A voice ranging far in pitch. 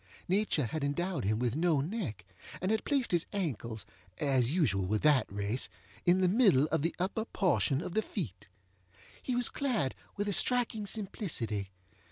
Yes: wide, 8.7 semitones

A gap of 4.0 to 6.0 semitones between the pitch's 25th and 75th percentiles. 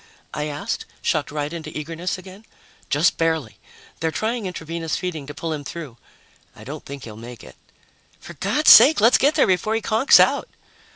Yes: average, 4.5 semitones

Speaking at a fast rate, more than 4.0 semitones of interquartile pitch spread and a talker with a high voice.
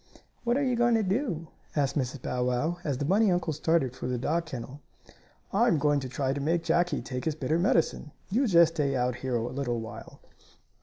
No: fast, 210 wpm; average, 5.2 semitones; medium, 150 Hz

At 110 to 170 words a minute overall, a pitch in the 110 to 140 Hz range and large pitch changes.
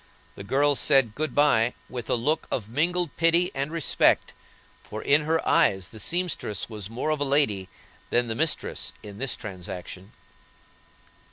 Yes: average, 160 wpm; low, 135 Hz; wide, 6.3 semitones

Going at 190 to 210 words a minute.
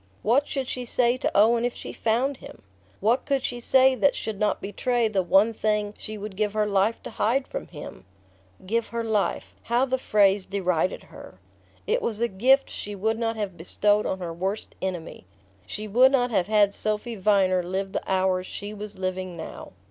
Yes: average, 195 wpm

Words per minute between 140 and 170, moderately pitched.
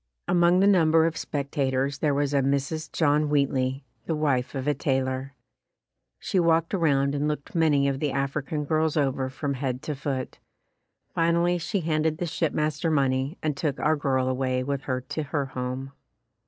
No: average, 180 wpm; medium, 145 Hz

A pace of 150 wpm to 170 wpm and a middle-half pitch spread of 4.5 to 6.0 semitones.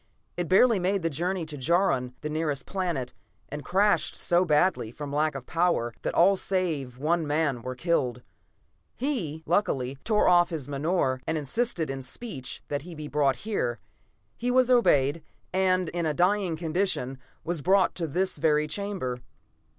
Yes: average, 165 wpm; average, 4.9 semitones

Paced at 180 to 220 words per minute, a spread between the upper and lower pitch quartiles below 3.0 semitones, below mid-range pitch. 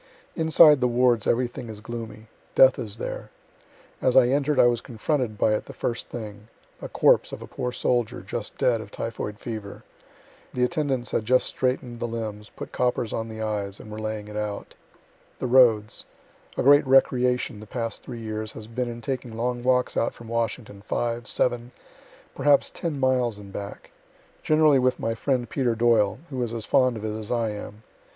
Yes: average, 190 wpm; narrow, 2.6 semitones; low, 120 Hz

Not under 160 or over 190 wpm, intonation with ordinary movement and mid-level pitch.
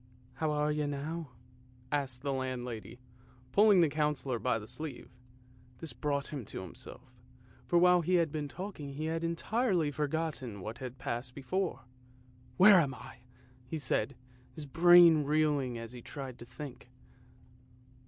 Yes: average, 165 wpm; average, 4.3 semitones; medium, 145 Hz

